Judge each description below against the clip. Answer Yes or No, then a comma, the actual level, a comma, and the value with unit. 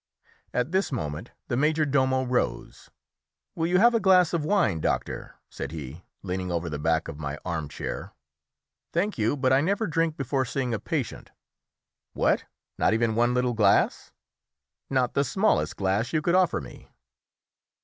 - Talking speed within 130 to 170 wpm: Yes, average, 165 wpm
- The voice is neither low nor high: No, low, 125 Hz